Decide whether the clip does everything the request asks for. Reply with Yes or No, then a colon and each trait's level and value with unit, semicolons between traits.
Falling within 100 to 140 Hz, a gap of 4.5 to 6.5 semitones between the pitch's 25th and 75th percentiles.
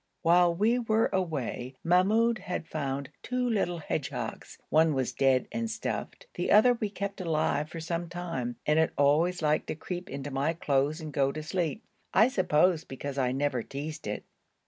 No: medium, 160 Hz; average, 4.9 semitones